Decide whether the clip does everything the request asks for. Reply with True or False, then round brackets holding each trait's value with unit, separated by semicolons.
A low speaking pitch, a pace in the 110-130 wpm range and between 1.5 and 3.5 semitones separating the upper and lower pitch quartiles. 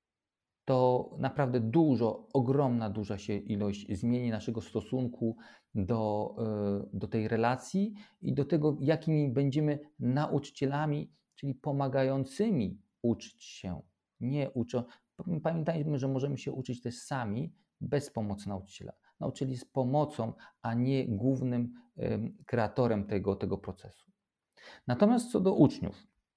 False (130 Hz; 115 wpm; 4.6 semitones)